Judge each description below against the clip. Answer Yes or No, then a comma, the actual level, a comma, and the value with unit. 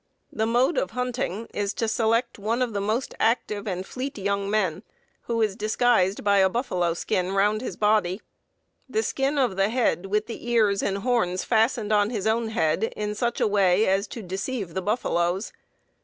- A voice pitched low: No, high, 210 Hz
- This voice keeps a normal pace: Yes, average, 185 wpm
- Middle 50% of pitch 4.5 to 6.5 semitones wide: No, average, 3.3 semitones